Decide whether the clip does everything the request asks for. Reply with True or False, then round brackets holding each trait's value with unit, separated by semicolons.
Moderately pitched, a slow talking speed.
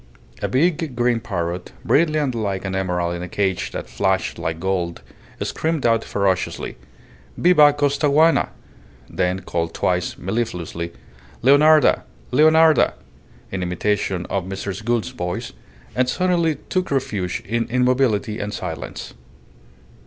False (110 Hz; 120 wpm)